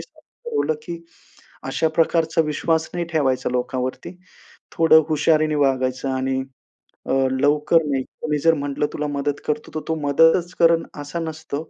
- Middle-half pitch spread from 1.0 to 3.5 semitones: Yes, narrow, 2.5 semitones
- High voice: No, medium, 150 Hz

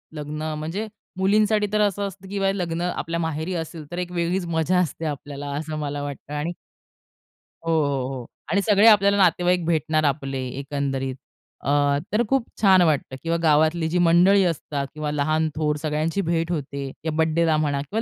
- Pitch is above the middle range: No, medium, 160 Hz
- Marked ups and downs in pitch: No, average, 3.4 semitones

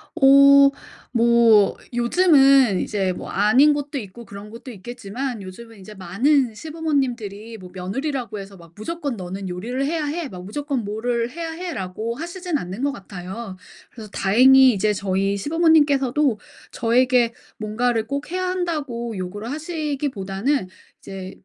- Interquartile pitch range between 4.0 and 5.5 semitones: No, wide, 5.9 semitones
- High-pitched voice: Yes, high, 235 Hz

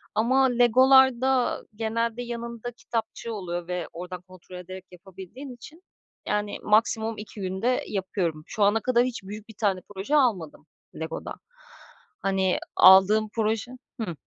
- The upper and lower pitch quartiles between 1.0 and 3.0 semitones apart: No, average, 4.2 semitones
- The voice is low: No, high, 215 Hz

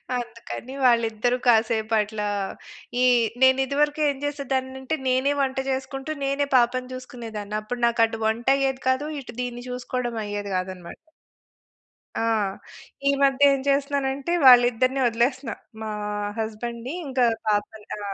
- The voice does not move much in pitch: No, average, 3.0 semitones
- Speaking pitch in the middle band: No, very high, 250 Hz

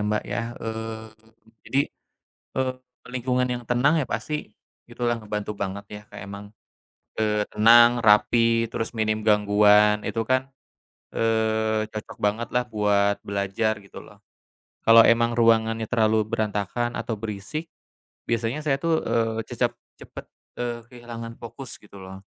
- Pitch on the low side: Yes, low, 115 Hz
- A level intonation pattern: Yes, narrow, 2.1 semitones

